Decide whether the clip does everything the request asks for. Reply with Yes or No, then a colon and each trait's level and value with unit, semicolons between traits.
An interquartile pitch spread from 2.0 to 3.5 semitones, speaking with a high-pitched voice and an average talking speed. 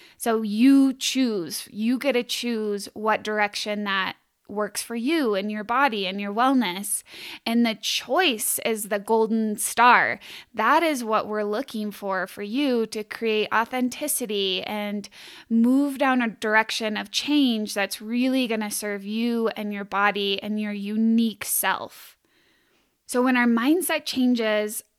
Yes: average, 3.1 semitones; high, 220 Hz; average, 150 wpm